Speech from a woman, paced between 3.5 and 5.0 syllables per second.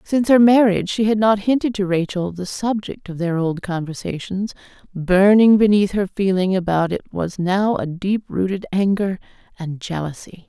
Yes: female; 4.9 syllables/s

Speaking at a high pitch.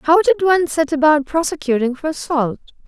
Yes: very high, 300 Hz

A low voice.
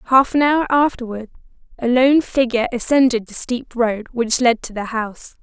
No: high, 245 Hz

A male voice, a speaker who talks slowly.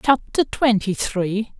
No: female; slow, 115 wpm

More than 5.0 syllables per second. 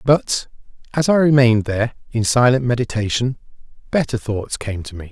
Yes: 5.5 syllables/s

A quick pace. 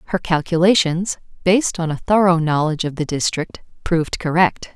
No: average, 150 wpm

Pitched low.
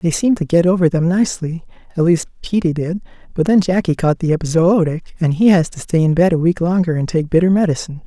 No: medium, 170 Hz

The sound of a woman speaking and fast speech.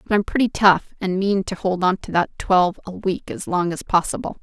Yes: female; fast, 230 wpm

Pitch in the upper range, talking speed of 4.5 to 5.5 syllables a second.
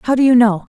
No: high, 240 Hz; 6.1 syllables/s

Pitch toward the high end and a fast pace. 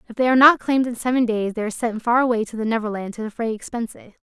Yes: high, 230 Hz; fast, 265 wpm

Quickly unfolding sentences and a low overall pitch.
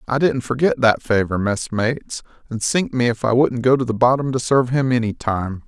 Yes: fast, 220 wpm; low, 120 Hz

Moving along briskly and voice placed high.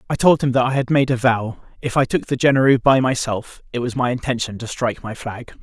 No: fast, 255 wpm; low, 125 Hz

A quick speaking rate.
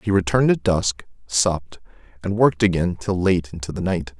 No: average, 185 wpm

